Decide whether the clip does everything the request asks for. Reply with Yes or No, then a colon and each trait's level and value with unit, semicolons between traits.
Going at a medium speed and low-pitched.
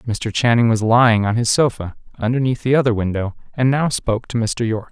No: fast, 210 wpm; low, 115 Hz